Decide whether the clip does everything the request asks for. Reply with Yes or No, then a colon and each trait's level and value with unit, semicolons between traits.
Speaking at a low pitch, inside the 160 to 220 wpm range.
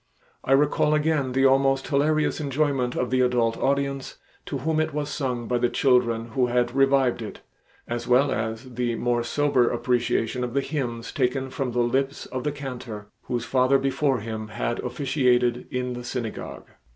Yes: low, 125 Hz; average, 175 wpm